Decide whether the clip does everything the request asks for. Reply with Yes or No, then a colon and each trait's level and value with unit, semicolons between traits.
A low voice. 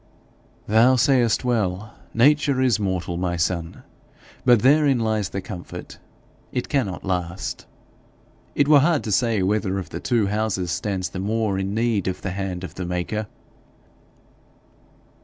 Yes: low, 105 Hz